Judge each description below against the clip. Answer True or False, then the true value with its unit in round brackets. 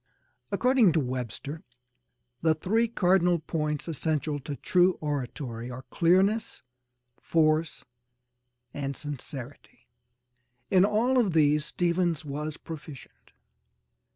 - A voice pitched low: False (155 Hz)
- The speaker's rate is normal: False (95 wpm)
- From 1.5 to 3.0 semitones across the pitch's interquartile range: False (3.8 semitones)